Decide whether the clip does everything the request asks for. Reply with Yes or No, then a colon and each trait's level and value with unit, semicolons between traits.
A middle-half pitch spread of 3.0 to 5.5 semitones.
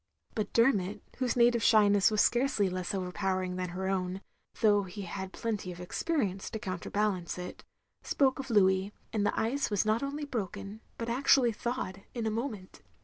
Yes: average, 3.9 semitones